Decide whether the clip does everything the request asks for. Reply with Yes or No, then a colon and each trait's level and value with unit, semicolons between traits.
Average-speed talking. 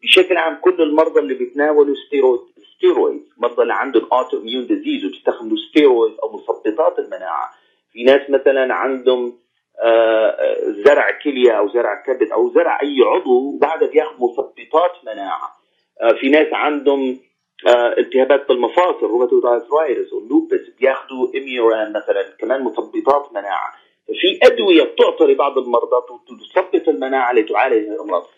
Yes: average, 125 wpm